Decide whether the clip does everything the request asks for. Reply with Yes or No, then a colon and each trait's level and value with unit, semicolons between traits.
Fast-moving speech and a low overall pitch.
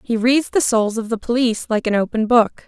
No: fast, 245 wpm; high, 230 Hz